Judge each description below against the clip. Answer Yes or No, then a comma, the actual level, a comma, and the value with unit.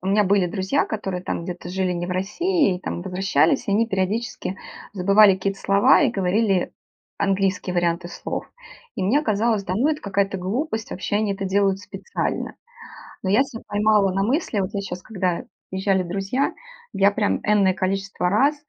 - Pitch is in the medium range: No, high, 195 Hz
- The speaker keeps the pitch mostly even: Yes, narrow, 2.3 semitones